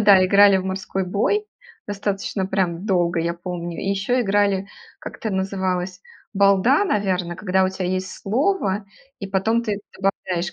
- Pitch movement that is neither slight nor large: No, narrow, 1.6 semitones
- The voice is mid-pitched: No, high, 195 Hz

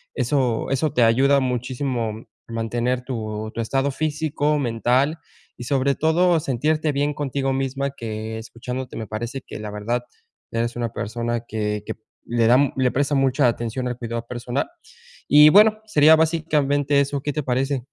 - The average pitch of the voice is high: No, low, 130 Hz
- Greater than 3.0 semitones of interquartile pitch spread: Yes, average, 3.5 semitones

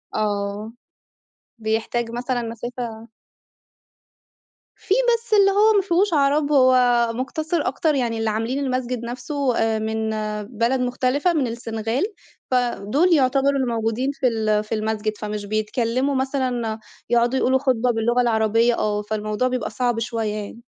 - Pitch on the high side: Yes, high, 240 Hz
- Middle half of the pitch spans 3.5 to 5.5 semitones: No, average, 3.1 semitones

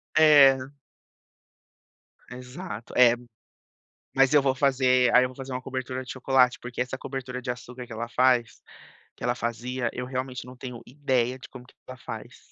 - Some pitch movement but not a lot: No, narrow, 1.1 semitones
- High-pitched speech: No, low, 125 Hz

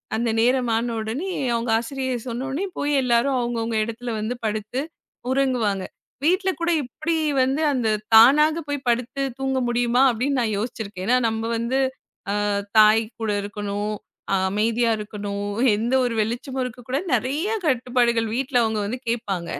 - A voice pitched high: Yes, high, 240 Hz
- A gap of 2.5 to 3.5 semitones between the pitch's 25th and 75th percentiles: Yes, average, 3.0 semitones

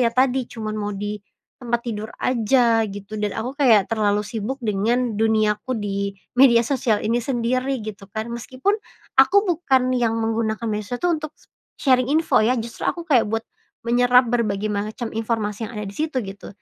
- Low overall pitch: No, high, 230 Hz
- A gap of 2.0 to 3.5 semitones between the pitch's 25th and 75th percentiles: Yes, average, 3.1 semitones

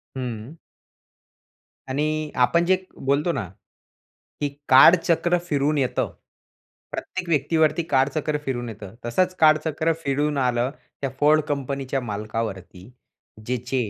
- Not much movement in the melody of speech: No, average, 3.9 semitones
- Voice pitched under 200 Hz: Yes, medium, 140 Hz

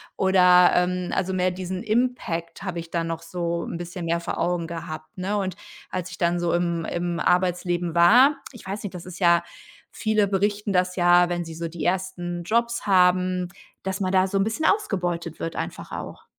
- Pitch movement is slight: Yes, narrow, 1.8 semitones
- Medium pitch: Yes, medium, 180 Hz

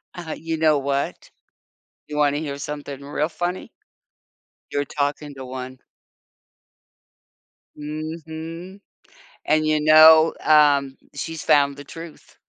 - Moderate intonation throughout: No, narrow, 2.0 semitones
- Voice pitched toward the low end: No, medium, 150 Hz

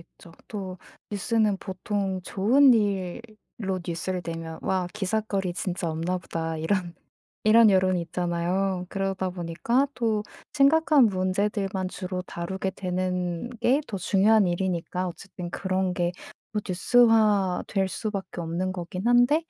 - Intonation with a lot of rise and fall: No, average, 2.9 semitones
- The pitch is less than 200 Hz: Yes, high, 190 Hz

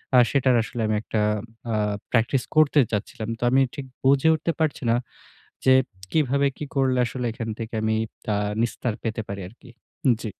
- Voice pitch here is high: No, low, 125 Hz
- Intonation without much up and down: No, average, 3.6 semitones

